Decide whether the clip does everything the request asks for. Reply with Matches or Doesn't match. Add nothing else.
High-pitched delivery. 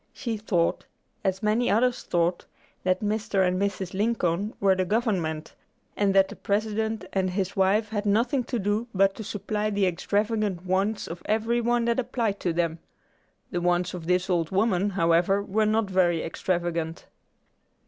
Matches